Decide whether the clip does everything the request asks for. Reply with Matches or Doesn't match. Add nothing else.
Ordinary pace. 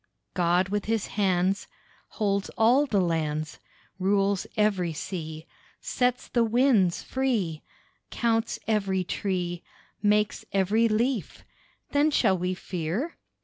Doesn't match